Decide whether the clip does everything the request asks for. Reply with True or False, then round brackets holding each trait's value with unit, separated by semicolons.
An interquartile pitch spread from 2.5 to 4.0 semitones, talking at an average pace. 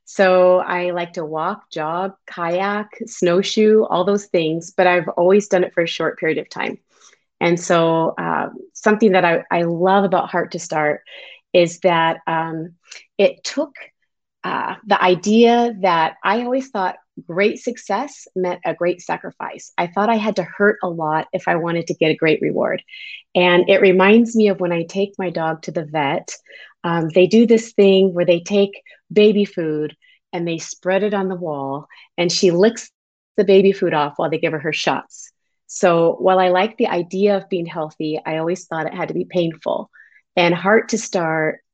True (3.2 semitones; 190 wpm)